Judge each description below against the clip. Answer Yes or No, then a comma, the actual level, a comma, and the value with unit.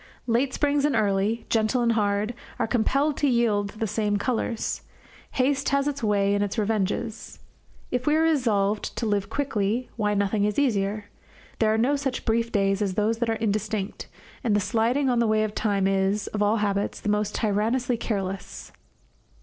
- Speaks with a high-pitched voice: Yes, high, 215 Hz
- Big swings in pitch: No, average, 2.9 semitones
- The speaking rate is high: No, average, 180 wpm